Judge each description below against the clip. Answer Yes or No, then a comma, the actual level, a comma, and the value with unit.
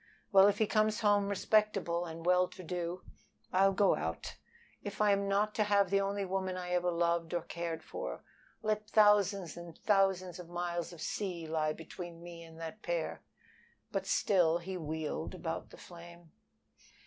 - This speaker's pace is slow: No, average, 170 wpm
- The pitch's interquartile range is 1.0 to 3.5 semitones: Yes, average, 2.9 semitones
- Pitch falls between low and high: Yes, medium, 180 Hz